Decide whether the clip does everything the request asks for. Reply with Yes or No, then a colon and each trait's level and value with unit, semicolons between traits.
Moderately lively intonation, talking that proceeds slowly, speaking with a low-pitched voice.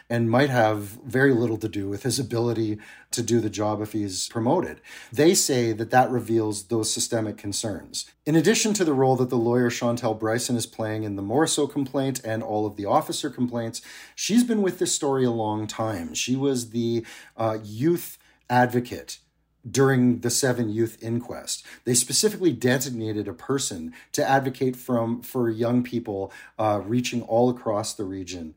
No: average, 3.3 semitones; average, 175 wpm; low, 120 Hz